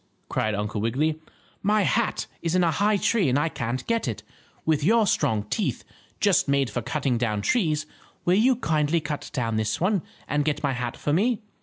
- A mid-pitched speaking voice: Yes, medium, 150 Hz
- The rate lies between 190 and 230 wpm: Yes, average, 195 wpm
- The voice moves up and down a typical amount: No, wide, 7.3 semitones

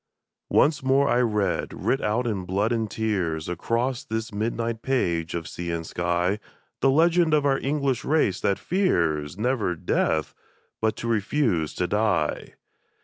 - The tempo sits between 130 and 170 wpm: Yes, average, 150 wpm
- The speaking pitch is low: Yes, low, 110 Hz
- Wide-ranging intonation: Yes, wide, 6.9 semitones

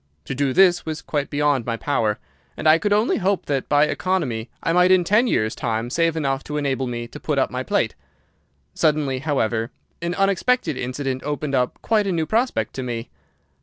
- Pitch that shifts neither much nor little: No, wide, 5.7 semitones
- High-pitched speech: No, medium, 145 Hz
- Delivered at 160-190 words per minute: No, average, 200 wpm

